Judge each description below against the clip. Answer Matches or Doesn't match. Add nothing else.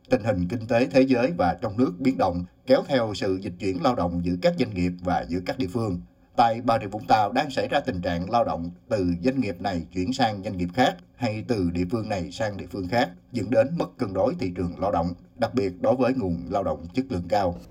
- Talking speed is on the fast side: Matches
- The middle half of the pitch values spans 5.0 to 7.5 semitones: Matches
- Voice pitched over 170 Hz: Doesn't match